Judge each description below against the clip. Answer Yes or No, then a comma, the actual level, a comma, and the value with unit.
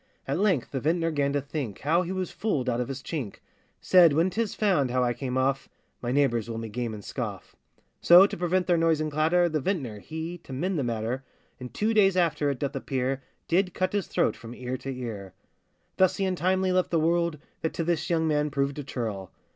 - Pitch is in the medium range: Yes, medium, 150 Hz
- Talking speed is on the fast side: Yes, fast, 225 wpm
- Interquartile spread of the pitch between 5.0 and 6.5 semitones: Yes, wide, 5.5 semitones